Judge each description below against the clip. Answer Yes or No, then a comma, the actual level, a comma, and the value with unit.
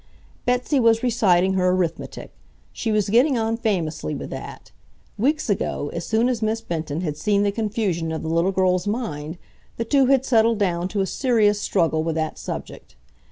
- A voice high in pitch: Yes, high, 205 Hz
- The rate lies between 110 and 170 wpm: No, average, 180 wpm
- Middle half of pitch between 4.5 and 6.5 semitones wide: Yes, average, 5.1 semitones